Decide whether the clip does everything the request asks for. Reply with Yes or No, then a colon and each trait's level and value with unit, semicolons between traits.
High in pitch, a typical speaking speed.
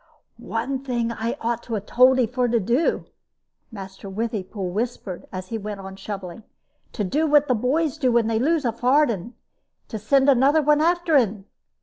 Yes: high, 235 Hz; average, 180 wpm